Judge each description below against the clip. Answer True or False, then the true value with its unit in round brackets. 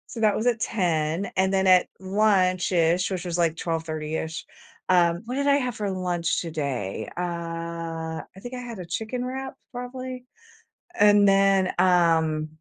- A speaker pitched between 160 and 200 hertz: True (185 Hz)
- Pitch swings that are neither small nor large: True (4.7 semitones)